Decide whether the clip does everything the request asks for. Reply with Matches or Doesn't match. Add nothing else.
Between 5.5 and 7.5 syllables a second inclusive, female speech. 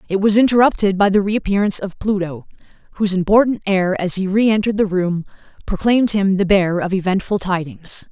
Matches